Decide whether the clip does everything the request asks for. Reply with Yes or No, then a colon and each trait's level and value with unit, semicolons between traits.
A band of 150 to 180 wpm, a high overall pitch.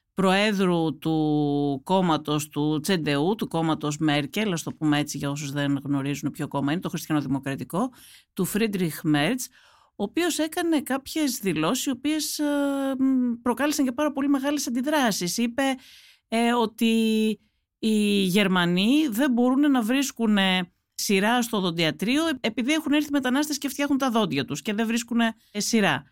No: average, 140 wpm; high, 220 Hz